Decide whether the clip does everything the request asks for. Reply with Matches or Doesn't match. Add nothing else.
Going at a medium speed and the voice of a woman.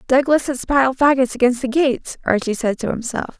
Matches